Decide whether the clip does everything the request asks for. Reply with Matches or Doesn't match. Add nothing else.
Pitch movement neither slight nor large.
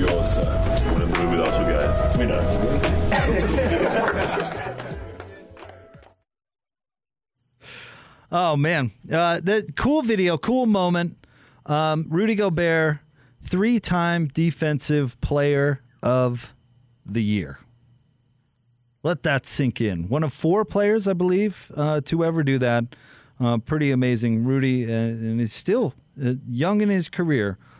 Doesn't match